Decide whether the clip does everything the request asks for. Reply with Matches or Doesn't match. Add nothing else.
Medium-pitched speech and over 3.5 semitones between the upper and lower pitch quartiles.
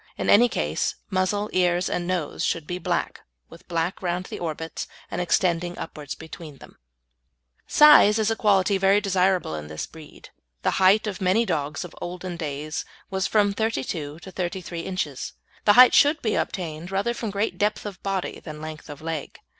Matches